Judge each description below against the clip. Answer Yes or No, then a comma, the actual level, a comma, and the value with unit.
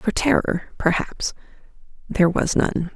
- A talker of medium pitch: Yes, medium, 180 Hz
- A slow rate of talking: Yes, slow, 100 wpm